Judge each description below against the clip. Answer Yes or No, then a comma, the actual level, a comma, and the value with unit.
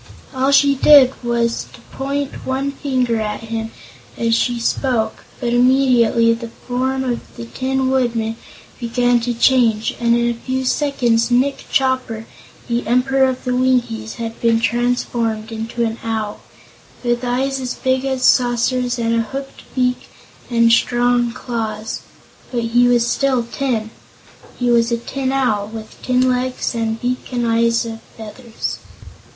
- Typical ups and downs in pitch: No, narrow, 2.1 semitones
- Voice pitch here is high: Yes, high, 240 Hz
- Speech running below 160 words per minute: Yes, average, 150 wpm